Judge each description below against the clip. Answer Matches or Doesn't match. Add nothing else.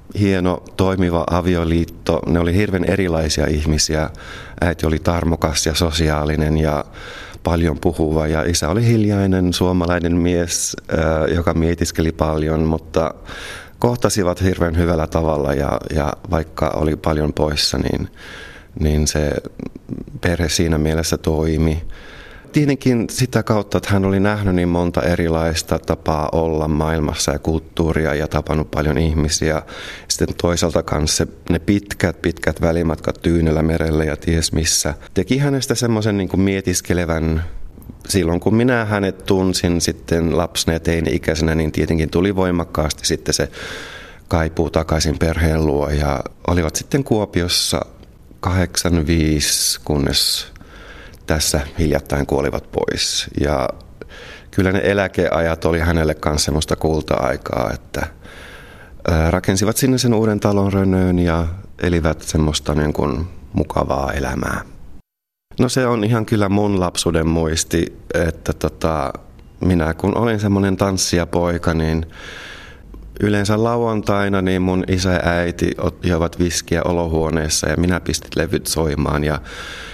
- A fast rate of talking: Doesn't match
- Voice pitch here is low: Matches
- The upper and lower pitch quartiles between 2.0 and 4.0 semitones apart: Matches